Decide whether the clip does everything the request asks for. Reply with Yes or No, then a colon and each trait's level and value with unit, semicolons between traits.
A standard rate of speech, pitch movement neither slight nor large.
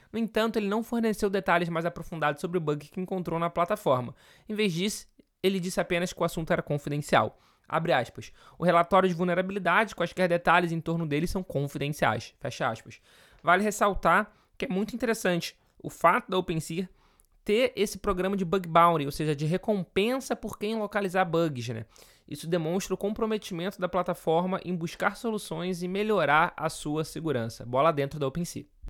Yes: average, 175 wpm; average, 3.5 semitones